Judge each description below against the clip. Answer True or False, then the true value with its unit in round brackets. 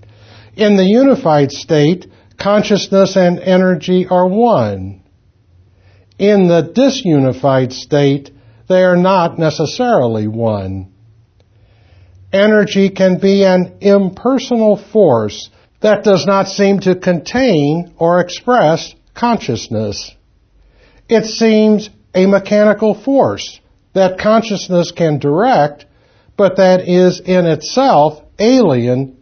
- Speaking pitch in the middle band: True (175 Hz)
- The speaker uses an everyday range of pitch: False (8.8 semitones)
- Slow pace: True (100 wpm)